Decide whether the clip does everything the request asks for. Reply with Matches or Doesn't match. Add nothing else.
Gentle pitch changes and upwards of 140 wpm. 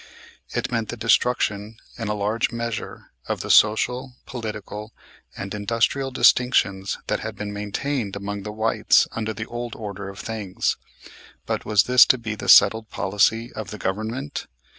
Matches